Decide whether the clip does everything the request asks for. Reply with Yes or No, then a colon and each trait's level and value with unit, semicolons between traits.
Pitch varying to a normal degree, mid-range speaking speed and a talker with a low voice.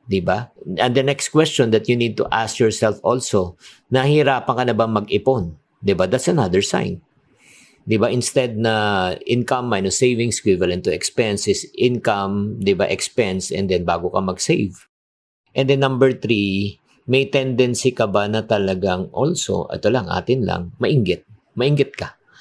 Yes: average, 4.7 semitones; average, 150 wpm; low, 115 Hz